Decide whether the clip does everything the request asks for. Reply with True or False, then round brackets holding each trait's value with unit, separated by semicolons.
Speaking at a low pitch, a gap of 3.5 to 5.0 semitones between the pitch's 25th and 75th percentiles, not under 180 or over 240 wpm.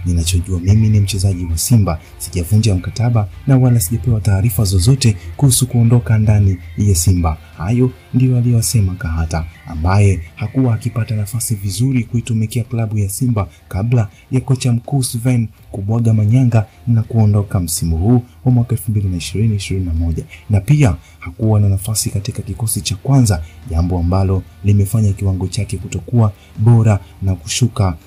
False (105 Hz; 4.1 semitones; 135 wpm)